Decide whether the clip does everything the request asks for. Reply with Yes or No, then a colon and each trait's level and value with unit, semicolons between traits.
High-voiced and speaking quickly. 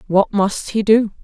No: high, 205 Hz; average, 195 wpm